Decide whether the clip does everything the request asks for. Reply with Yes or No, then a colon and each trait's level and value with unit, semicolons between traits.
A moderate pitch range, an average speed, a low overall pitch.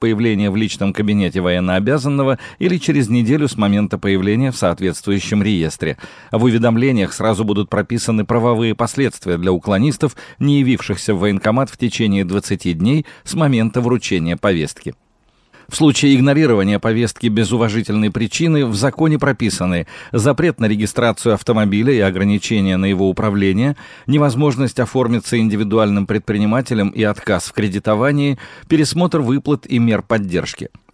Yes: average, 4.5 semitones; average, 130 wpm; low, 110 Hz